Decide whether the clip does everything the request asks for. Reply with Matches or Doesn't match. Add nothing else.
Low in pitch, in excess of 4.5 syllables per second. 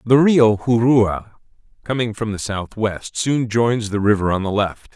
Doesn't match